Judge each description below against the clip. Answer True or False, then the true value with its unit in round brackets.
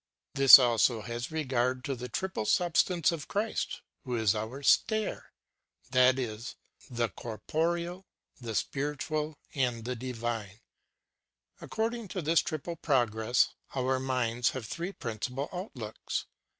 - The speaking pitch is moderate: False (130 Hz)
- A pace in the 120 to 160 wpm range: True (140 wpm)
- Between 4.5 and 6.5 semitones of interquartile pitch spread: True (5.3 semitones)